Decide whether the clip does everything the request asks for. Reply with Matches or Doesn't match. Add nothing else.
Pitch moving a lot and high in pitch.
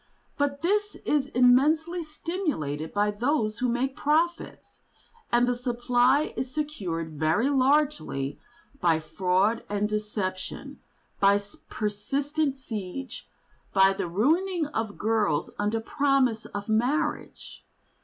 Matches